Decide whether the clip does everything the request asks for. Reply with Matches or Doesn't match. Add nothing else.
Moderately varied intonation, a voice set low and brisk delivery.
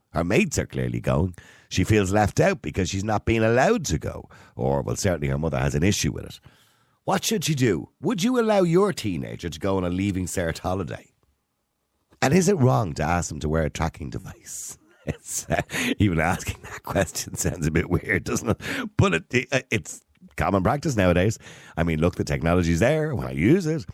Doesn't match